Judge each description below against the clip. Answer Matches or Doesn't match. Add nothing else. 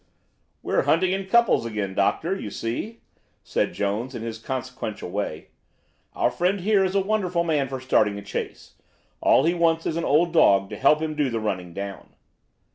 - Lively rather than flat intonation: Matches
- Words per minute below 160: Doesn't match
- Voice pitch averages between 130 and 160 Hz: Matches